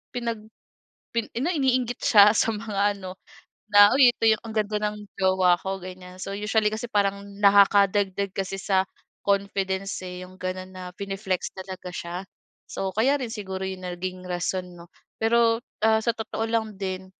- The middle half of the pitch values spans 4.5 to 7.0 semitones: No, average, 2.7 semitones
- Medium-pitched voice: No, high, 200 Hz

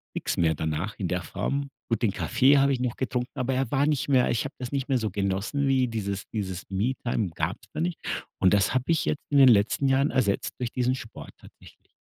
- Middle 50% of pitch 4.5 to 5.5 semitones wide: Yes, average, 5.1 semitones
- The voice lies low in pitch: Yes, low, 125 Hz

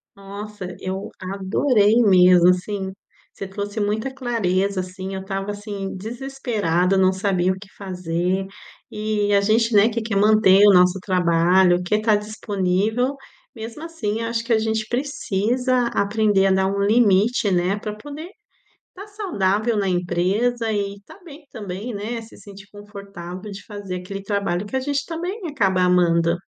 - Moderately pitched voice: No, high, 205 Hz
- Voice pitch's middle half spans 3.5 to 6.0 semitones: No, average, 3.1 semitones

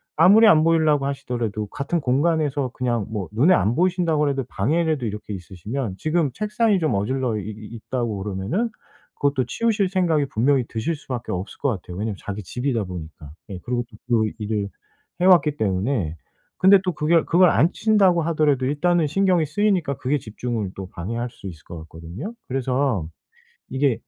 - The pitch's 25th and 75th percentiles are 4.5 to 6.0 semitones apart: No, wide, 7.5 semitones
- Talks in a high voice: No, low, 135 Hz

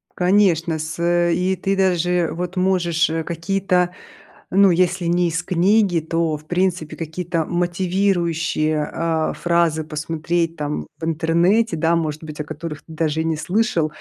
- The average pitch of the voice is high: No, medium, 170 Hz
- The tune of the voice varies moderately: No, narrow, 2.0 semitones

